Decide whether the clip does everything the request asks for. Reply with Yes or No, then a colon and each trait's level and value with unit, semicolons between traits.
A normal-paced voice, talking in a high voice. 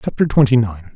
No: average, 190 wpm; low, 120 Hz